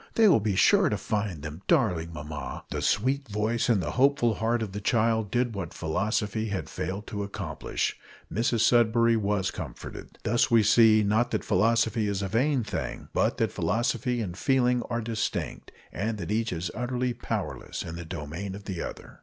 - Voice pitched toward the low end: Yes, low, 110 Hz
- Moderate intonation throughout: Yes, average, 3.4 semitones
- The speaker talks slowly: No, average, 185 wpm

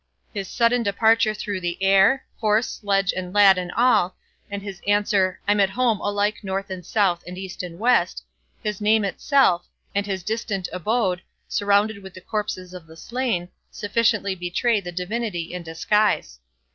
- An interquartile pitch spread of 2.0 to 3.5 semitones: Yes, average, 2.9 semitones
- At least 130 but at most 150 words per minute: No, average, 165 wpm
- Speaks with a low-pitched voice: No, high, 200 Hz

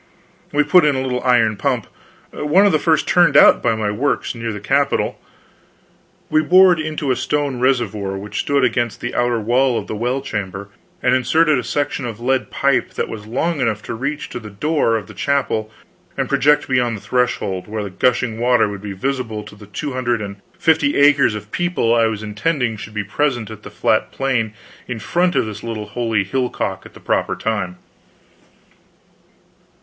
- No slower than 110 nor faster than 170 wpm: No, average, 195 wpm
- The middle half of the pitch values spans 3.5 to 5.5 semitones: Yes, average, 4.7 semitones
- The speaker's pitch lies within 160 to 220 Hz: No, low, 120 Hz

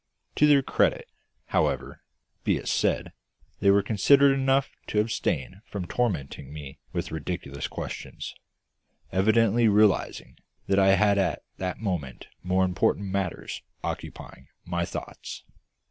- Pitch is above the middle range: No, low, 100 Hz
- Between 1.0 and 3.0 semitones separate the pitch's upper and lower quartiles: No, average, 3.8 semitones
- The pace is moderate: No, slow, 125 wpm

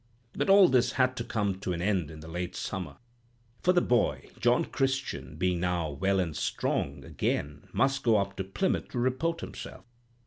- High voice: No, low, 100 Hz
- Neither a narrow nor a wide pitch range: No, wide, 7.0 semitones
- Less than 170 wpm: No, average, 185 wpm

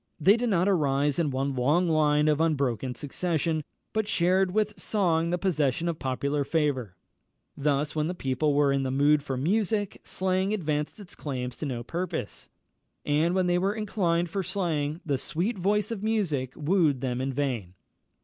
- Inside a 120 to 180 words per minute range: Yes, average, 175 wpm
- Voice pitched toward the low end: No, medium, 155 Hz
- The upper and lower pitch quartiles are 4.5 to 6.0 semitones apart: Yes, average, 4.8 semitones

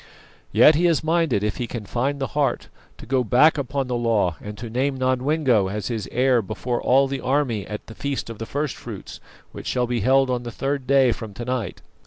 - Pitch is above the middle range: No, low, 125 Hz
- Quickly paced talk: Yes, fast, 225 wpm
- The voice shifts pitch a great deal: No, average, 3.2 semitones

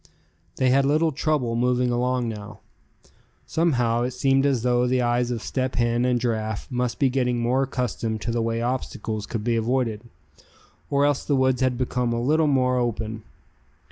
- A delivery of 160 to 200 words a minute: Yes, average, 175 wpm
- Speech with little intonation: Yes, narrow, 1.9 semitones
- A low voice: Yes, low, 125 Hz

